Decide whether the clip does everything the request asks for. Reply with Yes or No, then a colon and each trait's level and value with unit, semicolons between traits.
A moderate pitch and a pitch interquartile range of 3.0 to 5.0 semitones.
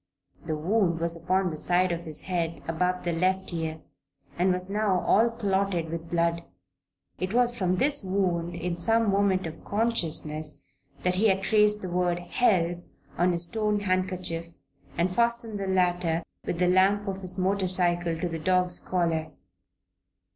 No: medium, 180 Hz; narrow, 2.5 semitones